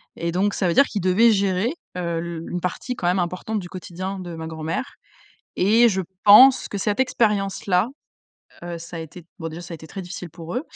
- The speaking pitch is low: No, medium, 180 Hz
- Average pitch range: Yes, average, 3.2 semitones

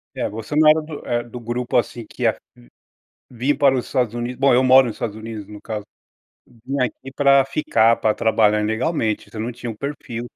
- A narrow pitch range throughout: No, average, 3.2 semitones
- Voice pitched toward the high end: No, low, 120 Hz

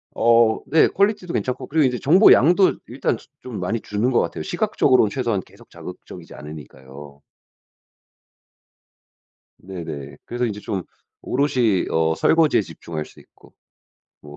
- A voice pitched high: No, low, 115 Hz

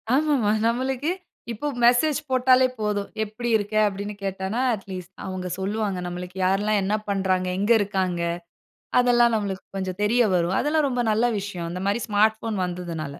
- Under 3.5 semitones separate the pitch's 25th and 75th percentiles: No, average, 4.1 semitones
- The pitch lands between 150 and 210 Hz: Yes, high, 205 Hz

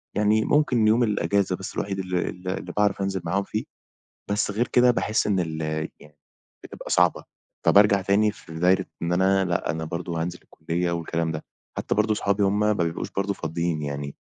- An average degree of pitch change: Yes, average, 3.6 semitones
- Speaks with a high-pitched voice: No, very low, 95 Hz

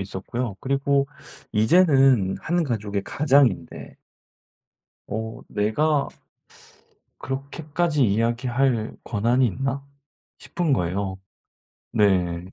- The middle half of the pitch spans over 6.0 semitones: No, average, 5.2 semitones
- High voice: No, low, 125 Hz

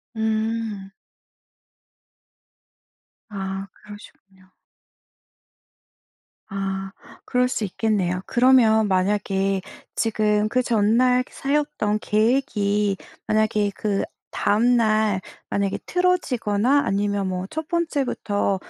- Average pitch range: Yes, average, 3.4 semitones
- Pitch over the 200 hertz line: Yes, high, 210 Hz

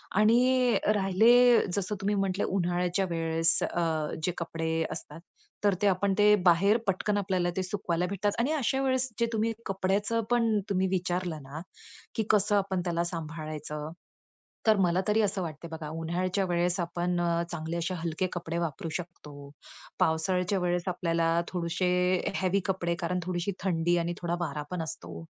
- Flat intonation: No, average, 3.0 semitones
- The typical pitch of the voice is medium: Yes, medium, 180 Hz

